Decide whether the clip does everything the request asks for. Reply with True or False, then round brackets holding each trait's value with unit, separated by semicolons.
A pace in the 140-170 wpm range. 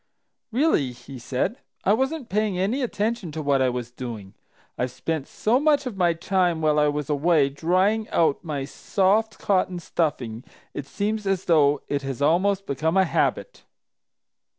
True (165 wpm)